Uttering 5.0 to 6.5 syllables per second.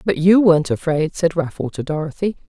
Yes: 5.7 syllables/s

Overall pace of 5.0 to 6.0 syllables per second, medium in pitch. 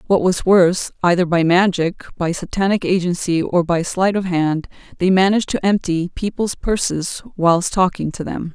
No: 4.8 syllables/s; medium, 180 Hz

